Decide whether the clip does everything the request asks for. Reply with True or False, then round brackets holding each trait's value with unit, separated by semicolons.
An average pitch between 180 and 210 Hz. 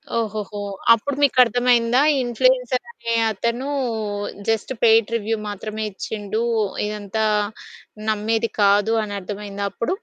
False (225 Hz)